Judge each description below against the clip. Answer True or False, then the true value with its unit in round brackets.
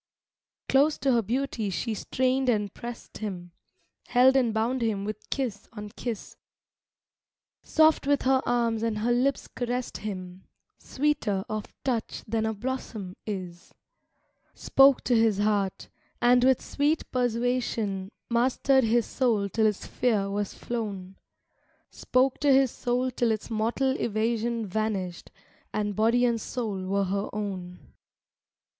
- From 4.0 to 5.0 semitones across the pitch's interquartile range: False (3.5 semitones)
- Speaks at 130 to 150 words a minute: True (140 wpm)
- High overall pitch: True (225 Hz)